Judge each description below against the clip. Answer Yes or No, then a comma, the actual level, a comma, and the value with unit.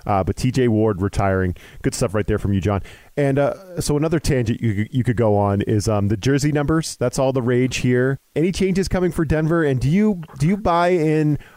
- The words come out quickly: Yes, fast, 230 wpm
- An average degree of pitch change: No, wide, 6.3 semitones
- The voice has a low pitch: Yes, low, 130 Hz